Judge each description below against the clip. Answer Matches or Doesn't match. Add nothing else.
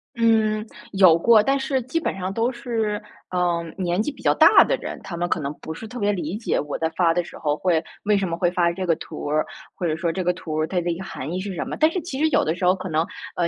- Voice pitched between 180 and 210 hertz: Matches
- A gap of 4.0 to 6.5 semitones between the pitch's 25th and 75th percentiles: Matches